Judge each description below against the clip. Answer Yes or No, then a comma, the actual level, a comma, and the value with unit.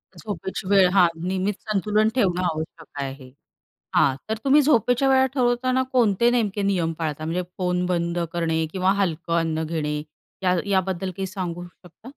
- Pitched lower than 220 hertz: Yes, medium, 185 Hz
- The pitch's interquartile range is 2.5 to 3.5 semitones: No, average, 4.1 semitones